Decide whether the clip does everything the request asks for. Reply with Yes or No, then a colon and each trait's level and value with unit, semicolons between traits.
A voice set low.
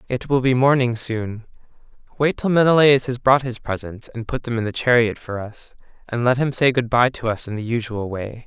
Yes: low, 120 Hz